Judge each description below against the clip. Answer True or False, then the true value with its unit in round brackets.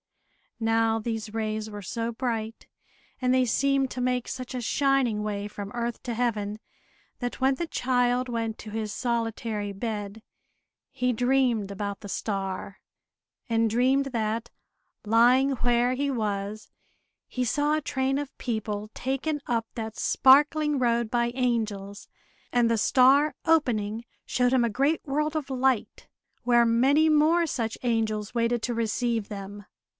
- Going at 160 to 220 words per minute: False (145 wpm)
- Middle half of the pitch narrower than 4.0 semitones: True (3.2 semitones)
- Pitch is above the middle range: True (235 Hz)